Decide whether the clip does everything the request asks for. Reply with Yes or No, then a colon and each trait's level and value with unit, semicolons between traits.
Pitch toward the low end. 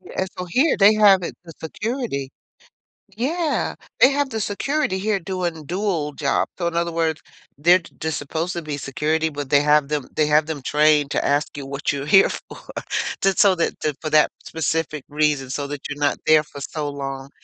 No: medium, 160 Hz